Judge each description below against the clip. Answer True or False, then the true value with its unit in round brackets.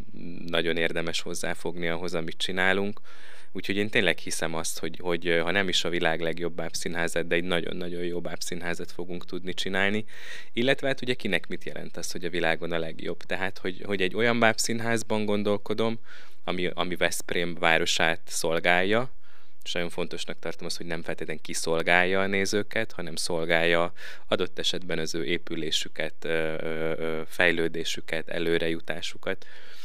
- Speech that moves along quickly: False (145 wpm)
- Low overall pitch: True (85 Hz)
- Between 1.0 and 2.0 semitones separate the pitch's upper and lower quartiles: False (2.8 semitones)